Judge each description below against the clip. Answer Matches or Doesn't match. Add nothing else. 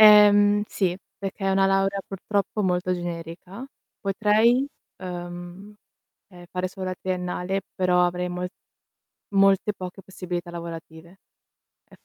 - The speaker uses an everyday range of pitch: Doesn't match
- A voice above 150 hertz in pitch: Matches